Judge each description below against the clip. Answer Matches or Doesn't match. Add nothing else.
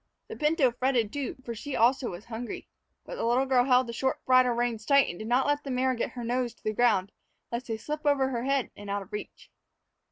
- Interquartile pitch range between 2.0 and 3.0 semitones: Matches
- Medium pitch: Doesn't match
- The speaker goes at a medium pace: Doesn't match